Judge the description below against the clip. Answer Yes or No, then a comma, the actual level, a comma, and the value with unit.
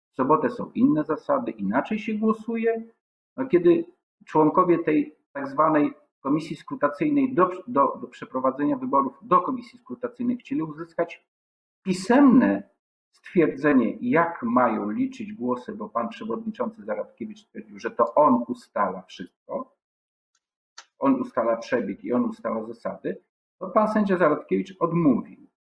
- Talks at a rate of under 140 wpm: Yes, average, 125 wpm